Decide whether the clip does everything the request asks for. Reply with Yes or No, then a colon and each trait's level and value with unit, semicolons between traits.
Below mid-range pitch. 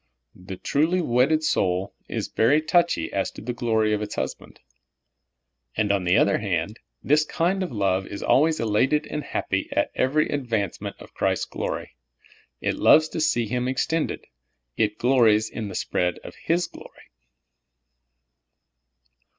Yes: low, 120 Hz